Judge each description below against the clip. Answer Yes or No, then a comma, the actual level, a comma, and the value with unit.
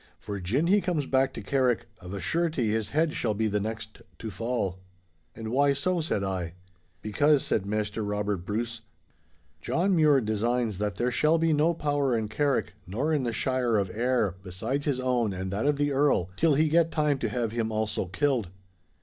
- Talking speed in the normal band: Yes, average, 190 wpm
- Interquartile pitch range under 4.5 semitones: No, wide, 5.6 semitones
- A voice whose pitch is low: Yes, low, 120 Hz